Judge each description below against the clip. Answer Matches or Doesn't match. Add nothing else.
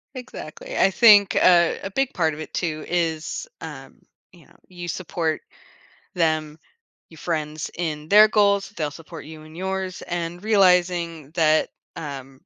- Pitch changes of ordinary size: Matches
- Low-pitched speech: Doesn't match